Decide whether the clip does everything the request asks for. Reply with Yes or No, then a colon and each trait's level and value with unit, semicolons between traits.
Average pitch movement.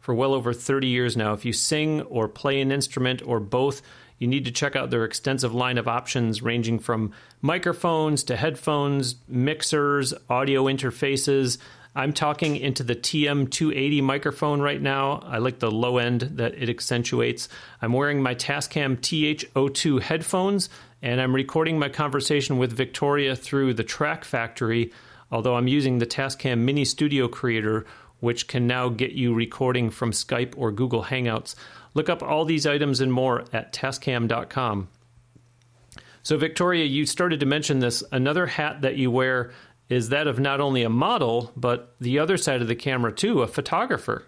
Yes: average, 3.0 semitones